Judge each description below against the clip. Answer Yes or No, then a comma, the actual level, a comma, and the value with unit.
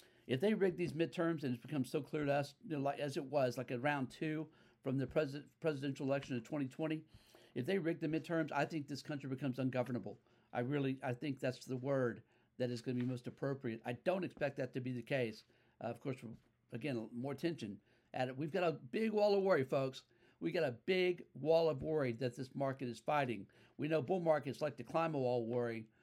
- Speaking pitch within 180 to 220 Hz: No, low, 135 Hz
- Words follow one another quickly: Yes, fast, 235 wpm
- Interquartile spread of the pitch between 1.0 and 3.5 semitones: No, average, 4.0 semitones